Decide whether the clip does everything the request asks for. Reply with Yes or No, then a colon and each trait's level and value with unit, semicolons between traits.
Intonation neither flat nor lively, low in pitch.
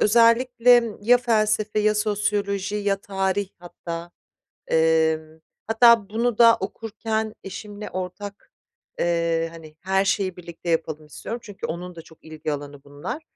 No: average, 4.6 semitones; high, 200 Hz